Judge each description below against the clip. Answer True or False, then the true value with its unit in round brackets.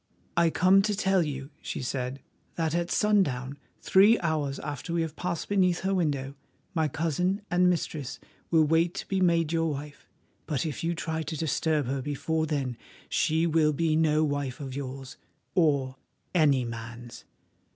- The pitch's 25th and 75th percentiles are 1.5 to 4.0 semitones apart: True (3.6 semitones)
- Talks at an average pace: True (165 wpm)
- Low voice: False (155 Hz)